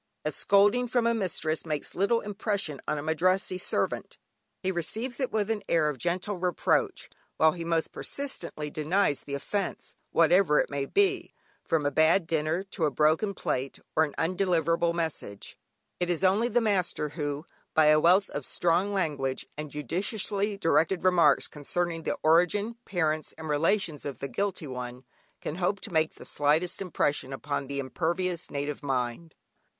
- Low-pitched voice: No, medium, 165 Hz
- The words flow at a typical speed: Yes, average, 165 wpm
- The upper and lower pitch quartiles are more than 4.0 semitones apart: Yes, average, 4.5 semitones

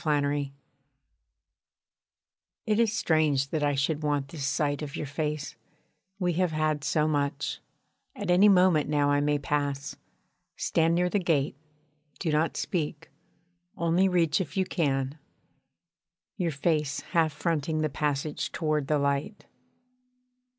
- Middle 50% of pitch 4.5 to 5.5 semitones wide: No, average, 2.7 semitones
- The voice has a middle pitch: Yes, medium, 150 Hz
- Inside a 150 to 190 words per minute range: No, slow, 135 wpm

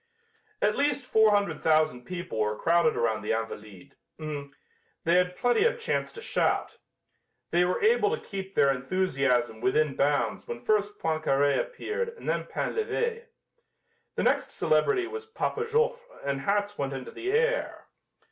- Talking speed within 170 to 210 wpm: No, average, 150 wpm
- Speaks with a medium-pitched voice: Yes, medium, 180 Hz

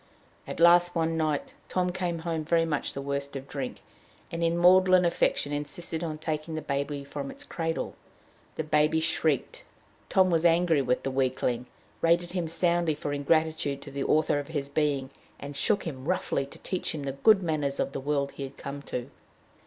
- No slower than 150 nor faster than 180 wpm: No, average, 190 wpm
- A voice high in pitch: No, medium, 155 Hz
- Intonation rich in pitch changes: No, average, 3.2 semitones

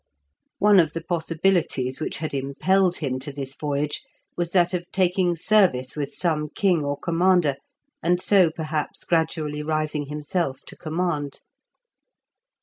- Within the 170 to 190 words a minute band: No, average, 140 wpm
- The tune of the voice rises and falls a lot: No, average, 3.3 semitones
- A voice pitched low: No, medium, 160 Hz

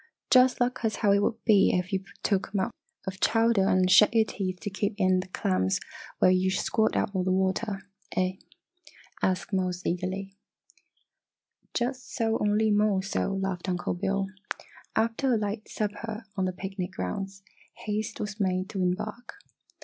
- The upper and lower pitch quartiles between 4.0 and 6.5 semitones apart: No, narrow, 2.5 semitones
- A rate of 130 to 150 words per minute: No, average, 170 wpm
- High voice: Yes, high, 195 Hz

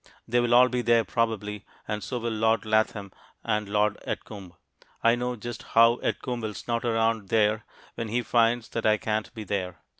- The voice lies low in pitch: Yes, low, 115 Hz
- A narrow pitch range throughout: Yes, narrow, 1.8 semitones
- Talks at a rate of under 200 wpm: Yes, average, 185 wpm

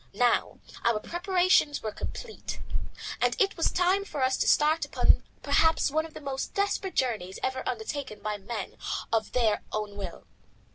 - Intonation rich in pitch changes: Yes, wide, 8.1 semitones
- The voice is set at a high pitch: Yes, very high, 265 Hz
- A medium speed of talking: Yes, average, 160 wpm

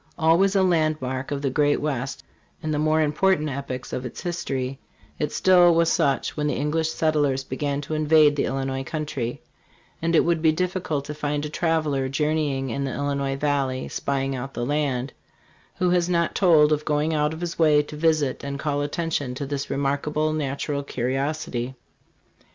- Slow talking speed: No, average, 180 wpm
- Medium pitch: Yes, medium, 150 Hz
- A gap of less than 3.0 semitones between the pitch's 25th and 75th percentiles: Yes, narrow, 2.4 semitones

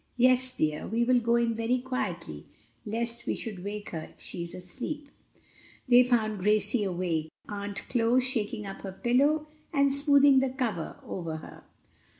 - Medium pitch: No, high, 230 Hz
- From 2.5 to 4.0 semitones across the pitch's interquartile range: No, average, 4.7 semitones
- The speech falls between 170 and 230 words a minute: No, average, 160 wpm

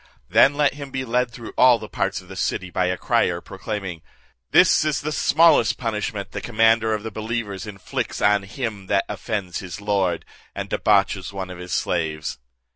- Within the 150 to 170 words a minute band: No, average, 180 wpm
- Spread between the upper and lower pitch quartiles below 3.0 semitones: No, average, 3.9 semitones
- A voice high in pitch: No, low, 105 Hz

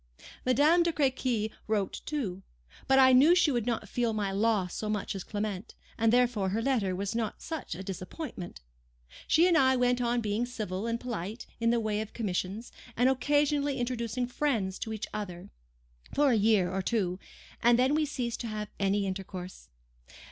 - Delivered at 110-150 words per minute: No, average, 180 wpm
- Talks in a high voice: Yes, high, 230 Hz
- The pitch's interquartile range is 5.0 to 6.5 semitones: No, average, 4.2 semitones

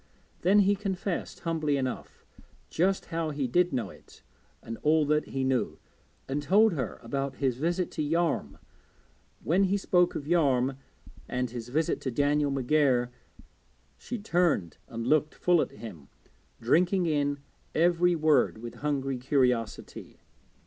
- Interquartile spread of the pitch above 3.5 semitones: Yes, average, 5.0 semitones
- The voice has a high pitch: No, medium, 150 Hz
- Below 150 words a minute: Yes, average, 140 wpm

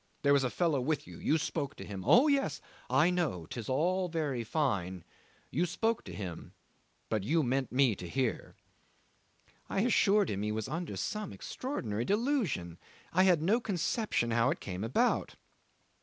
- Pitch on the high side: No, medium, 145 Hz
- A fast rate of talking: No, average, 170 wpm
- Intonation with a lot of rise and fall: Yes, wide, 8.4 semitones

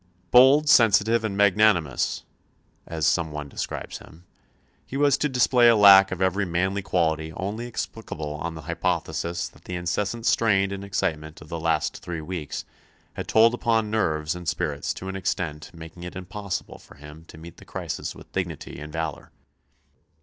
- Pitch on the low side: Yes, very low, 90 Hz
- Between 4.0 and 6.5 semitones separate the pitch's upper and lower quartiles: Yes, average, 4.5 semitones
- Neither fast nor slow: Yes, average, 170 wpm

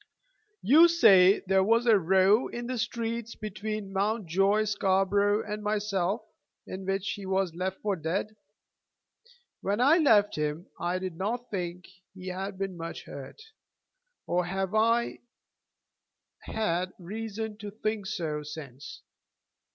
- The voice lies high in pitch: Yes, high, 195 Hz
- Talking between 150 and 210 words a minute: No, slow, 135 wpm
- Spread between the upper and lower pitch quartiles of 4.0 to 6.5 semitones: No, average, 2.8 semitones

